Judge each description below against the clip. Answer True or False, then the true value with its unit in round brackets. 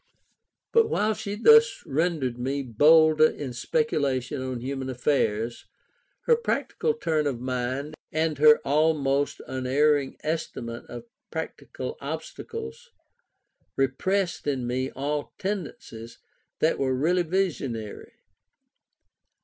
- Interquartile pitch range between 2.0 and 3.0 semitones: False (4.1 semitones)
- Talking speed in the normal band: False (105 wpm)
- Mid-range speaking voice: True (145 Hz)